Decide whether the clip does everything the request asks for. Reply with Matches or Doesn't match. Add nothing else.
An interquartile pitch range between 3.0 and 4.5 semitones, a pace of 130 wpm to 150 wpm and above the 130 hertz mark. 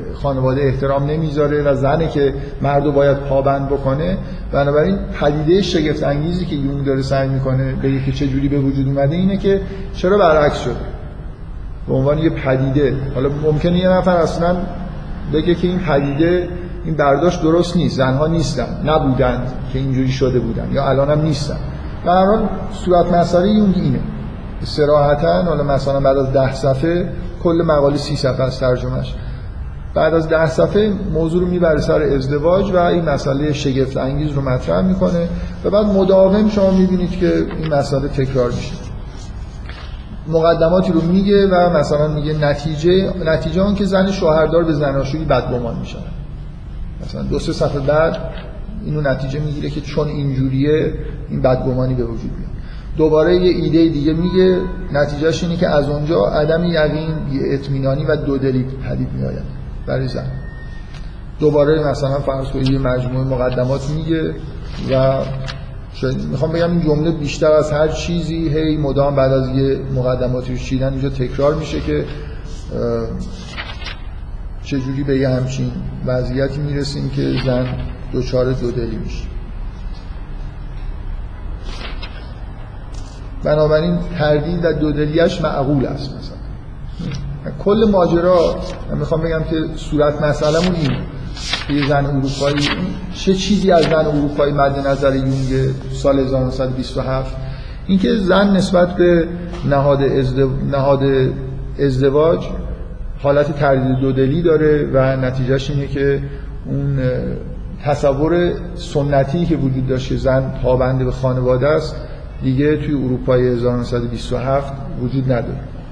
Matches